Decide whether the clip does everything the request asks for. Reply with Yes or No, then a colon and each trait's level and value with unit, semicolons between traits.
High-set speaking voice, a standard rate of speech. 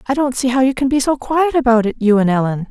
No: very high, 250 Hz; fast, 290 wpm